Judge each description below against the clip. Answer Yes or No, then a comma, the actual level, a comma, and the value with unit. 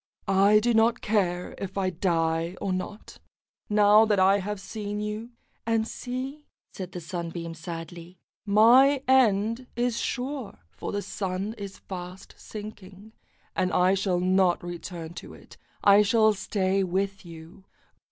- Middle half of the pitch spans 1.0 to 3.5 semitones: Yes, average, 3.2 semitones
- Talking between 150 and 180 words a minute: No, average, 140 wpm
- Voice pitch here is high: Yes, high, 195 Hz